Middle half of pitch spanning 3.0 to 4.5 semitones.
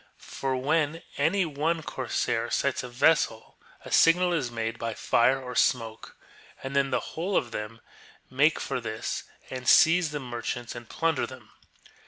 No: average, 5.1 semitones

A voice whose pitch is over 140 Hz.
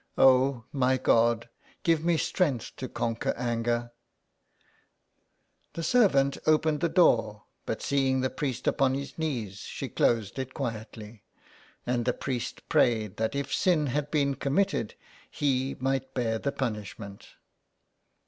No: low, 130 Hz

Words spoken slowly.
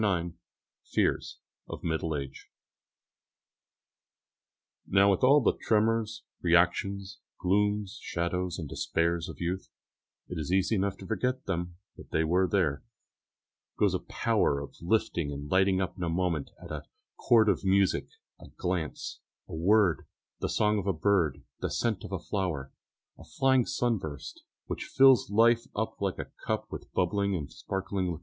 No: average, 155 wpm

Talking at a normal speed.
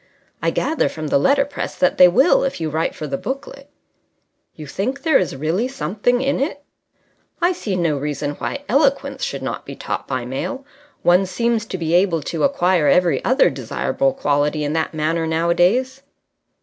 Yes: average, 175 wpm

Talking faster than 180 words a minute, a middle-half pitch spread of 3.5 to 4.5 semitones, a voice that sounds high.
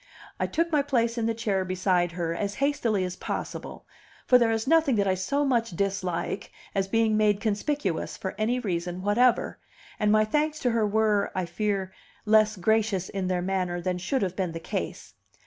Yes: average, 190 wpm; average, 3.8 semitones; high, 210 Hz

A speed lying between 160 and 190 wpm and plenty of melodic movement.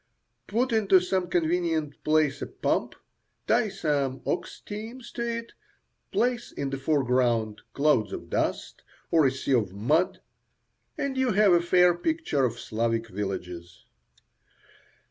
No: slow, 135 wpm; wide, 8.7 semitones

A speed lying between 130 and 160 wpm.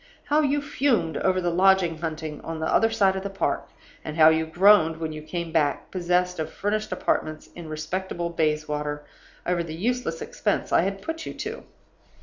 No: average, 185 wpm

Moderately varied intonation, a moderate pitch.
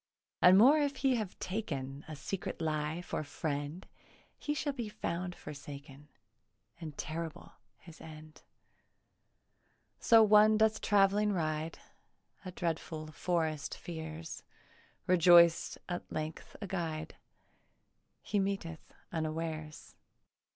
Yes: average, 4.0 semitones; medium, 165 Hz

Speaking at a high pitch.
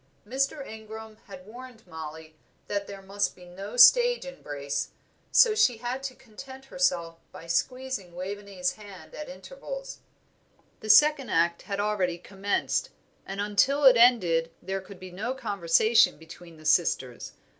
Yes: high, 205 Hz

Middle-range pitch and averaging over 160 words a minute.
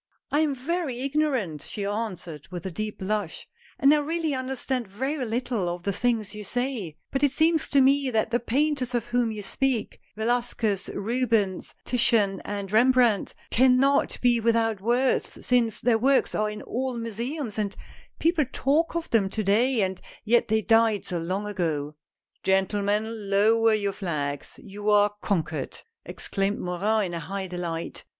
No: high, 225 Hz; average, 170 wpm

